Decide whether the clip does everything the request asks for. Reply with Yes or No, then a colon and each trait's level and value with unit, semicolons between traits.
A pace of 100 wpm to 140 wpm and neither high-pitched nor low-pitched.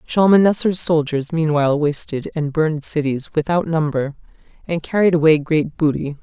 Yes: slow, 135 wpm; medium, 155 Hz